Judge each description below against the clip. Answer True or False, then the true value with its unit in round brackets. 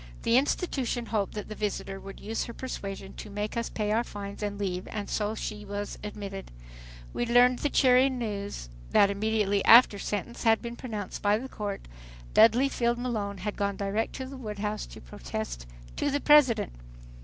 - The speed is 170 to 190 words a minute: True (185 wpm)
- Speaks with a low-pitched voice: False (210 Hz)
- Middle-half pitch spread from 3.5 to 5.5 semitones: False (3.0 semitones)